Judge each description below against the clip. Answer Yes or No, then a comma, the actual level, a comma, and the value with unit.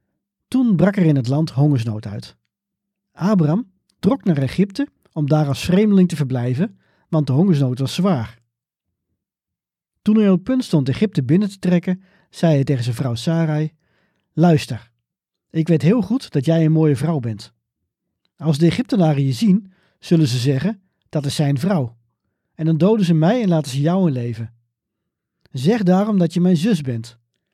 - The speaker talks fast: No, average, 175 wpm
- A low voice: No, medium, 160 Hz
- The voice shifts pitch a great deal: Yes, wide, 5.7 semitones